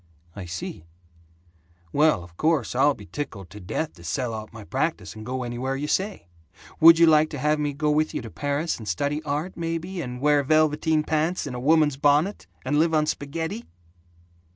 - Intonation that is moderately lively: Yes, average, 4.4 semitones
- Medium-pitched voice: Yes, medium, 145 Hz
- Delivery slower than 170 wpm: No, average, 195 wpm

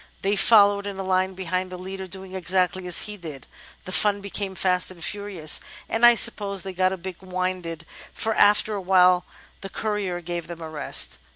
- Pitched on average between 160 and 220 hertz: Yes, medium, 185 Hz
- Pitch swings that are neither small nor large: No, narrow, 1.9 semitones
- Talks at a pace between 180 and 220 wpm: Yes, average, 195 wpm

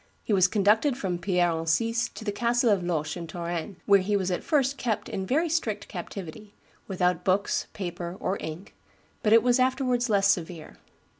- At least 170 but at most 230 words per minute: Yes, average, 180 wpm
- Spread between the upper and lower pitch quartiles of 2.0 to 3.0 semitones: No, average, 4.5 semitones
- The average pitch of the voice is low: No, high, 200 Hz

